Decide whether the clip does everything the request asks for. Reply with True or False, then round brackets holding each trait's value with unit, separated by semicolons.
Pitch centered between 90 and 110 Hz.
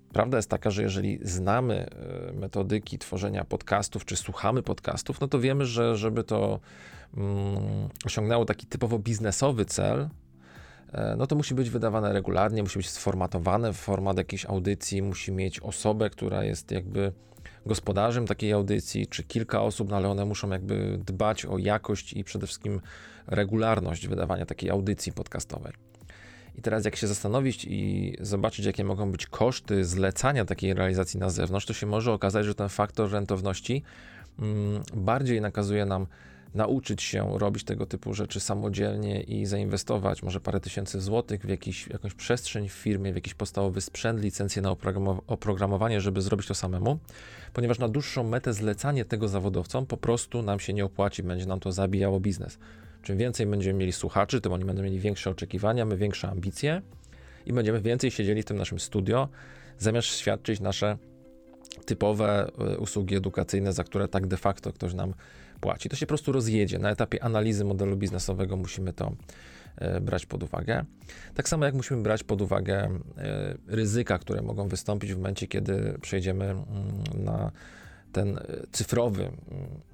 True (100 Hz)